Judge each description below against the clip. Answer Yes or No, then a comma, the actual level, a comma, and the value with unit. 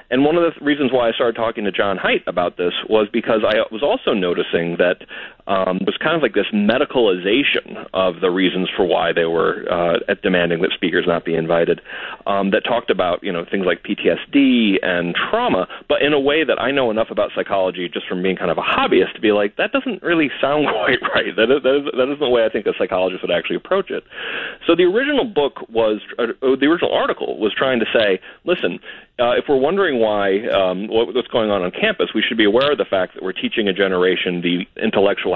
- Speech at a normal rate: No, fast, 230 wpm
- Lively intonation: Yes, wide, 7.4 semitones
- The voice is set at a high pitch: No, low, 100 Hz